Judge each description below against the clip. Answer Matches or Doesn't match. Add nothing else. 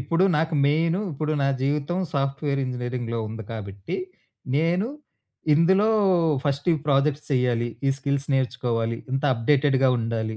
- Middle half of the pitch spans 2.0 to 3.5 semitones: Doesn't match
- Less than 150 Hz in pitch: Matches